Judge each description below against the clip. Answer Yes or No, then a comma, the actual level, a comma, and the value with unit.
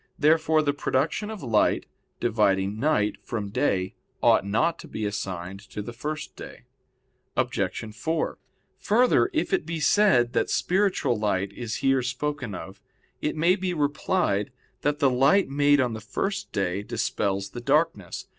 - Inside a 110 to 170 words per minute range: Yes, average, 155 wpm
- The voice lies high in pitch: No, low, 130 Hz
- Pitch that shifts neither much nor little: No, wide, 7.3 semitones